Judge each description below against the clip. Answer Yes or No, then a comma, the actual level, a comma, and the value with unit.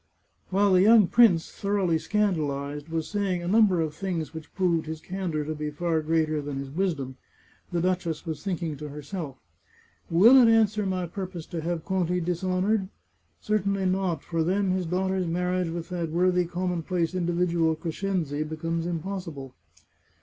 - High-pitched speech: No, medium, 175 Hz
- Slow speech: No, average, 165 wpm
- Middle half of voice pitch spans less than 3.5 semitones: Yes, average, 2.9 semitones